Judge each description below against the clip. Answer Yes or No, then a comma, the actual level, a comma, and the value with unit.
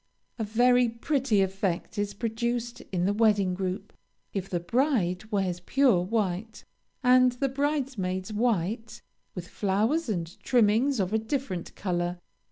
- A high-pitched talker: Yes, high, 215 Hz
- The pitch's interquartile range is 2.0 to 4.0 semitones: No, average, 4.7 semitones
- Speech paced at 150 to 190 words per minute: No, slow, 135 wpm